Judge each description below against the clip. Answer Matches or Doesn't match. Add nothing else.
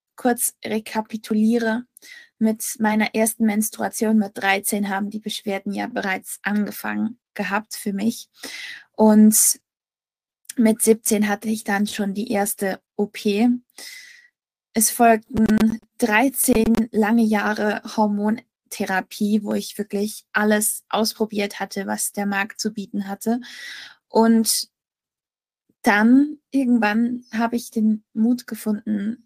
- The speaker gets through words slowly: Matches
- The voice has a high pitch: Matches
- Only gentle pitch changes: Matches